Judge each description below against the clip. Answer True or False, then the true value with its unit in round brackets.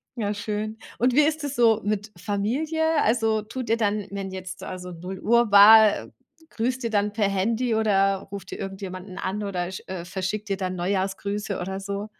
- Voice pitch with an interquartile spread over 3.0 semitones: False (2.6 semitones)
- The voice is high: True (205 Hz)